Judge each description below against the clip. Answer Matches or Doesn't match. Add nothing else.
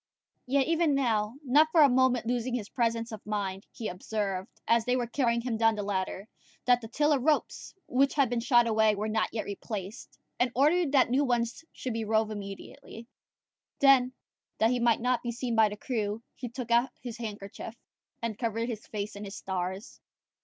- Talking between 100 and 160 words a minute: Doesn't match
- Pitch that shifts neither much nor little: Matches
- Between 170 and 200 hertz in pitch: Doesn't match